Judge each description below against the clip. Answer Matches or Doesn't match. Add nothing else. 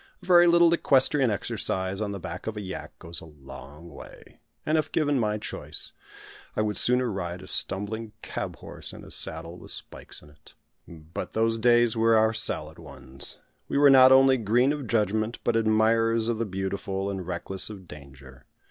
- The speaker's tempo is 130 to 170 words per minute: Doesn't match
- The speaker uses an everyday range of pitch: Matches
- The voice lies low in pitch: Matches